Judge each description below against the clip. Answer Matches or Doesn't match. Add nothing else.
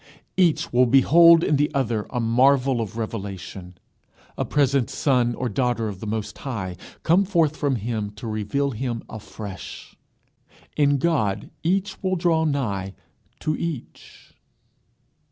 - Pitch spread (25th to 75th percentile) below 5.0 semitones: Doesn't match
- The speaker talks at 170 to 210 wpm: Doesn't match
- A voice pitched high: Doesn't match